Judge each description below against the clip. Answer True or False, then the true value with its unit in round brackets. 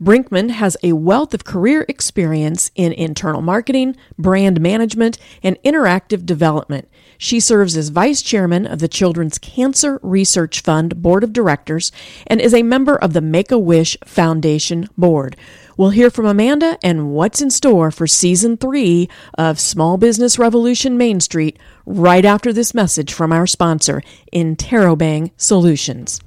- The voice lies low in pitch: False (180 Hz)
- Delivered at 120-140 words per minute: False (150 wpm)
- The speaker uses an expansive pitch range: True (6.1 semitones)